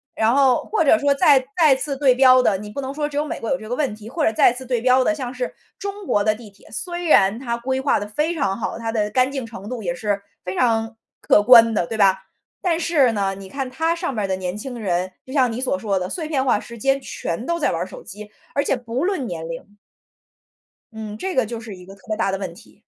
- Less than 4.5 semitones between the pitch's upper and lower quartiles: No, average, 4.8 semitones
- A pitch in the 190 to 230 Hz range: No, high, 240 Hz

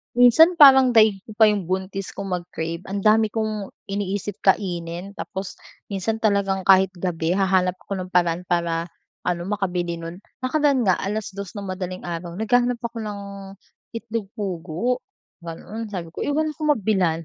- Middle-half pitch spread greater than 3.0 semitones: Yes, average, 3.4 semitones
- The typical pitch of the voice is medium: No, high, 195 Hz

